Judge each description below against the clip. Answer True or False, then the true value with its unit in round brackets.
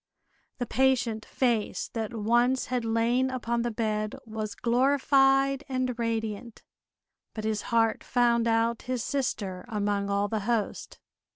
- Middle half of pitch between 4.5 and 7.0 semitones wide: False (2.6 semitones)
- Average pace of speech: False (130 wpm)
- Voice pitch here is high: True (235 Hz)